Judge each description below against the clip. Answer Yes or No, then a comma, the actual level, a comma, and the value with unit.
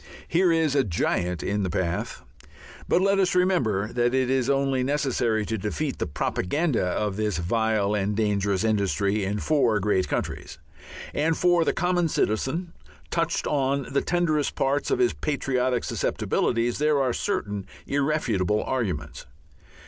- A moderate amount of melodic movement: No, wide, 6.7 semitones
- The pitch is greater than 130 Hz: No, low, 125 Hz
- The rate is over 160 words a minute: No, average, 150 wpm